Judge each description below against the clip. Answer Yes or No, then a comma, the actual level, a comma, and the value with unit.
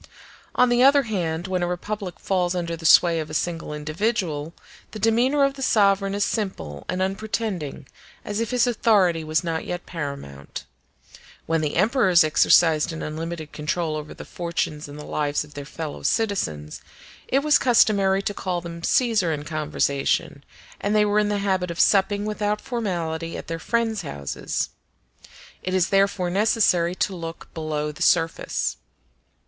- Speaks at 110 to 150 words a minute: No, average, 165 wpm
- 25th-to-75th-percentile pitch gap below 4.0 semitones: No, average, 4.8 semitones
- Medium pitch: Yes, medium, 180 Hz